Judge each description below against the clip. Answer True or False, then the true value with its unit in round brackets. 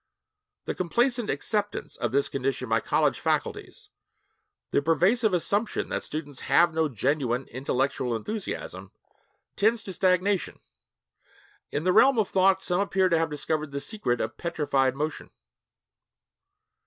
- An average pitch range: False (6.3 semitones)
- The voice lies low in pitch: False (160 Hz)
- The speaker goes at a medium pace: False (130 wpm)